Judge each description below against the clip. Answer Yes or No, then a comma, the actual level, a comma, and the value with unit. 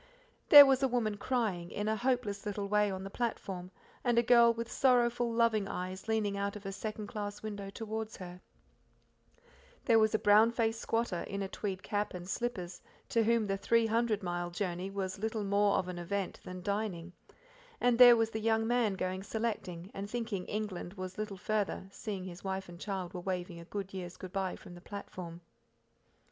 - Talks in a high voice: Yes, high, 205 Hz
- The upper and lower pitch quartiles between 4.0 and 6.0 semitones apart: No, average, 3.3 semitones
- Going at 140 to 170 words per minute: No, average, 190 wpm